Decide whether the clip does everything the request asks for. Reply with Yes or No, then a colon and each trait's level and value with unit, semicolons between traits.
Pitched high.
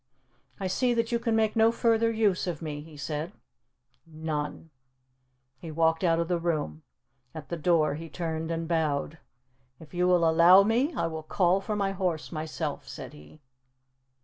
No: medium, 165 Hz